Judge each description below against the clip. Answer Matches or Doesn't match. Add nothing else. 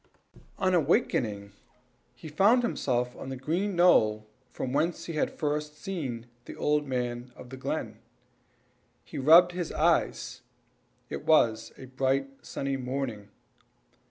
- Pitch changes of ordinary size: Matches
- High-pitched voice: Doesn't match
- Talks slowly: Matches